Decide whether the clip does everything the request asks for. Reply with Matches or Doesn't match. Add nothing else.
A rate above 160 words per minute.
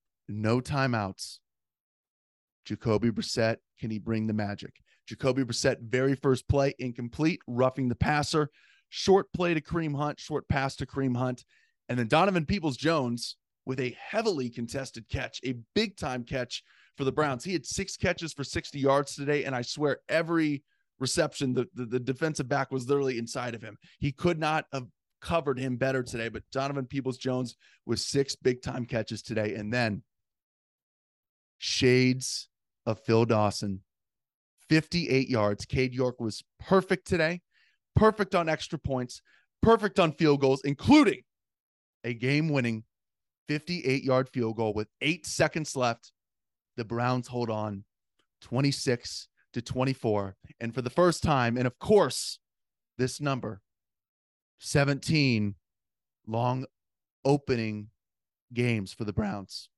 Doesn't match